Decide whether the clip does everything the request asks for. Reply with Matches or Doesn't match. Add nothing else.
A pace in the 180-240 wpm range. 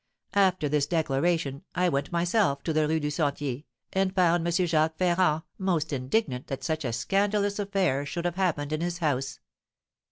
Doesn't match